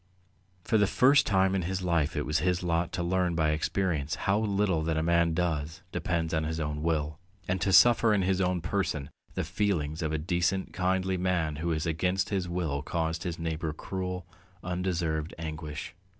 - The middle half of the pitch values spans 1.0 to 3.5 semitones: Yes, average, 2.9 semitones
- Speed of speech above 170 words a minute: Yes, average, 190 wpm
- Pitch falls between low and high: No, very low, 85 Hz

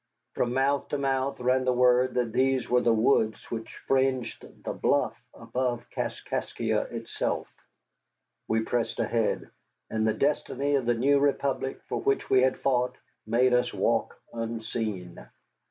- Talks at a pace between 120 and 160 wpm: Yes, average, 145 wpm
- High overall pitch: No, low, 125 Hz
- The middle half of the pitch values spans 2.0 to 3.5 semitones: Yes, narrow, 2.4 semitones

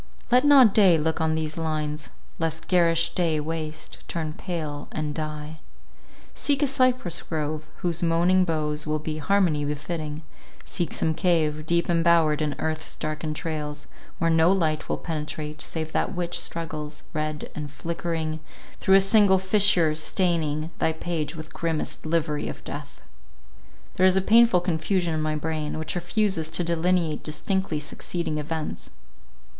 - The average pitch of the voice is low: No, medium, 160 Hz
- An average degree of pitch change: No, narrow, 2.3 semitones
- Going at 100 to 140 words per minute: No, average, 150 wpm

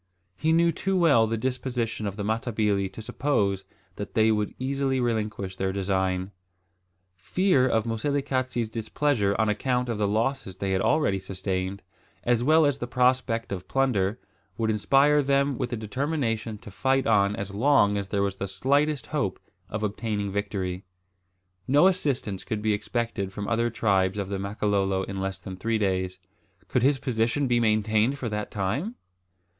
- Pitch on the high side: No, low, 110 Hz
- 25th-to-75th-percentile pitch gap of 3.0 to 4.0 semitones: No, average, 4.6 semitones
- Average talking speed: Yes, average, 170 wpm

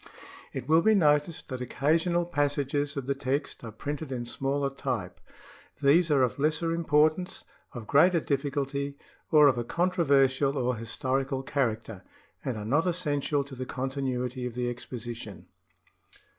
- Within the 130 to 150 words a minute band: Yes, average, 145 wpm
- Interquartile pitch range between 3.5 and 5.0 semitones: No, average, 2.9 semitones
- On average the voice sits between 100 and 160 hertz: Yes, medium, 140 Hz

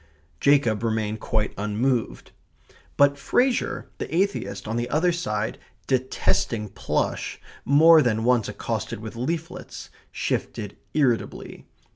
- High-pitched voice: No, low, 120 Hz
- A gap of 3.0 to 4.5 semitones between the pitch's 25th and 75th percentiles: No, average, 5.1 semitones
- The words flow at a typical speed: No, slow, 110 wpm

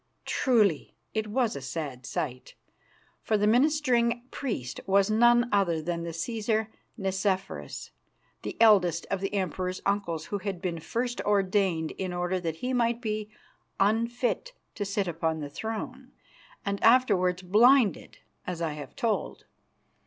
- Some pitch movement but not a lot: Yes, average, 4.7 semitones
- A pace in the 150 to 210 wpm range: No, average, 140 wpm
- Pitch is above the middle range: Yes, high, 200 Hz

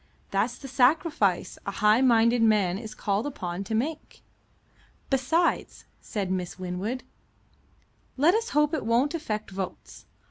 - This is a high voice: Yes, high, 230 Hz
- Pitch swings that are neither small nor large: No, wide, 5.7 semitones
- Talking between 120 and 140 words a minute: Yes, slow, 135 wpm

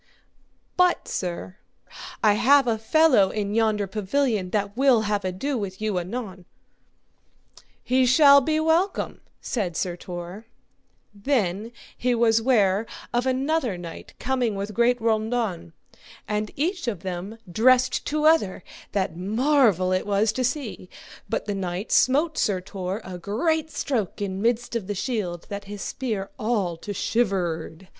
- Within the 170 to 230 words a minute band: No, average, 145 wpm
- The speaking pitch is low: No, high, 215 Hz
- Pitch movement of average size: Yes, average, 4.9 semitones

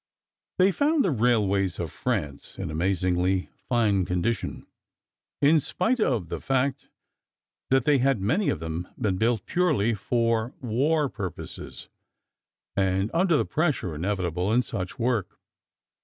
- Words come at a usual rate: No, slow, 130 wpm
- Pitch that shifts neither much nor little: No, wide, 6.9 semitones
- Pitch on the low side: Yes, low, 115 Hz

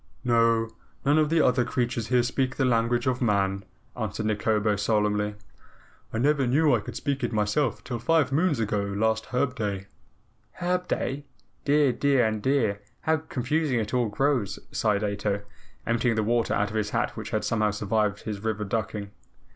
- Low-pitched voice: Yes, low, 115 Hz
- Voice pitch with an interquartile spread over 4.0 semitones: No, average, 3.7 semitones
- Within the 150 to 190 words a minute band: Yes, average, 175 wpm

